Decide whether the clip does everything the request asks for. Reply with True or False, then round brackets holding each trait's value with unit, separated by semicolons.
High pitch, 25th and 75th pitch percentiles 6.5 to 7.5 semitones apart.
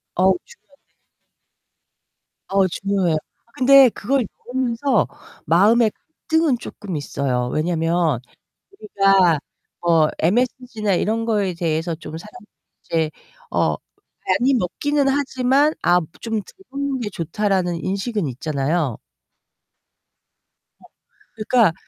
True (200 Hz; 6.8 semitones)